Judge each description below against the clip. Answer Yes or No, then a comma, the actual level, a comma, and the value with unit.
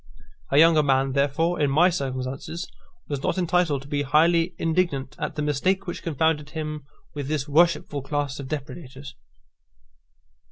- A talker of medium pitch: Yes, medium, 150 Hz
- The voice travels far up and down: No, average, 3.1 semitones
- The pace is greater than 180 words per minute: No, average, 150 wpm